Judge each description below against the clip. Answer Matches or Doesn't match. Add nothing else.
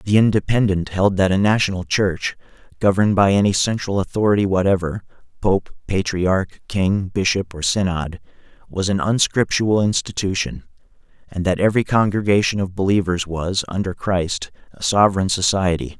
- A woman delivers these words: Doesn't match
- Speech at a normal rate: Doesn't match